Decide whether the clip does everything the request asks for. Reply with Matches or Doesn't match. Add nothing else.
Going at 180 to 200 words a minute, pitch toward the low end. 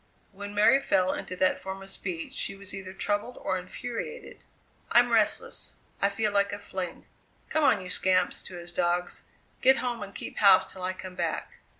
Doesn't match